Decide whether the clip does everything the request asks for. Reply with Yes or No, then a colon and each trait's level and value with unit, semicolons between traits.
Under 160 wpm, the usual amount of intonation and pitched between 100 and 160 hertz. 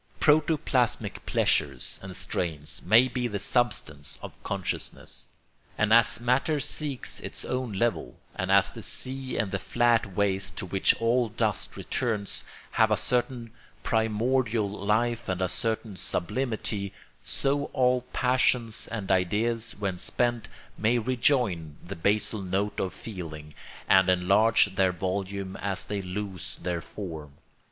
Yes: slow, 135 wpm; average, 4.1 semitones; low, 105 Hz